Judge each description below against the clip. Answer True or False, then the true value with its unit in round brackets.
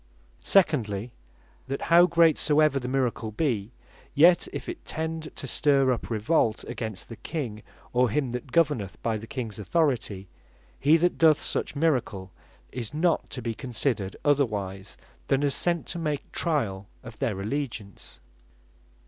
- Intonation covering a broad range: True (6.0 semitones)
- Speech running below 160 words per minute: True (150 wpm)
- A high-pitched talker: False (130 Hz)